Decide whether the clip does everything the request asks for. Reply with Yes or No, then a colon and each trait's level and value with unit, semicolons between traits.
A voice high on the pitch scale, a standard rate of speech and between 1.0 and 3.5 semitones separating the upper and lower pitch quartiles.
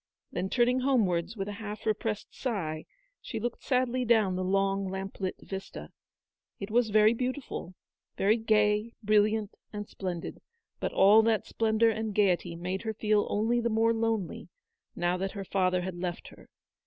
Yes: high, 210 Hz; average, 170 wpm; average, 2.8 semitones